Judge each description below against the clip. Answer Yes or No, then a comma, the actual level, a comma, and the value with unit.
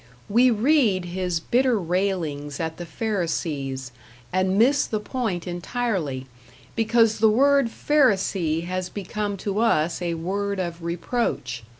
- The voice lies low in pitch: No, high, 190 Hz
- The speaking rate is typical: No, slow, 125 wpm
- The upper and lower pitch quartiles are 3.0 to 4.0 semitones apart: No, average, 5.0 semitones